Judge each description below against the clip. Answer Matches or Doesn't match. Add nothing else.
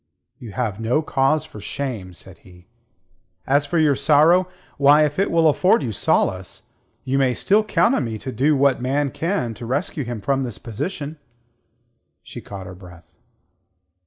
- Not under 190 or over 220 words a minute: Doesn't match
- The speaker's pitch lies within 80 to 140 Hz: Matches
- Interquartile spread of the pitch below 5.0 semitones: Doesn't match